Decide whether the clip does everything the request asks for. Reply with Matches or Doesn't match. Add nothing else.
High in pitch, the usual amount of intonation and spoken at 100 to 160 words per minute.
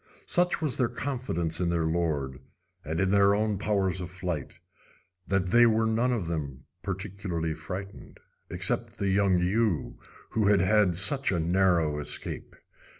Doesn't match